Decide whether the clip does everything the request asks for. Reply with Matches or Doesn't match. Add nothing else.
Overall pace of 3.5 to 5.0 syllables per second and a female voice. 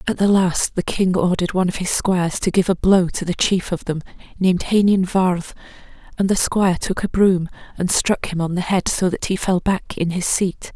Doesn't match